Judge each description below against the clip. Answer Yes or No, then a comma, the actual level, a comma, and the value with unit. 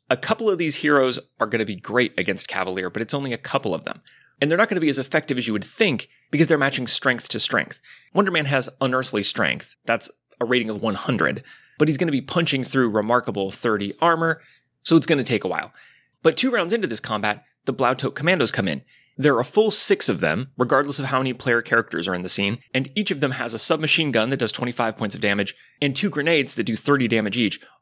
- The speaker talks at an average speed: No, fast, 235 wpm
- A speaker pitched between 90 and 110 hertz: No, low, 135 Hz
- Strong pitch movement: Yes, wide, 5.9 semitones